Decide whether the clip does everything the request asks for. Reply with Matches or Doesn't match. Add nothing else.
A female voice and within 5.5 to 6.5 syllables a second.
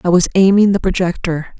Matches